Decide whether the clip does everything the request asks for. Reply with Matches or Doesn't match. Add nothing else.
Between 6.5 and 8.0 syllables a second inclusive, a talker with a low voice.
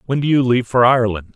Matches